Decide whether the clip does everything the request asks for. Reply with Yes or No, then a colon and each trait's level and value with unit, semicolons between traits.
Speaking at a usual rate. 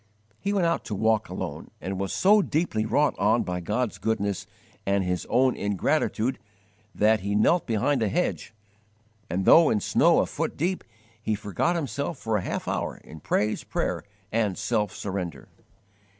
Yes: average, 165 wpm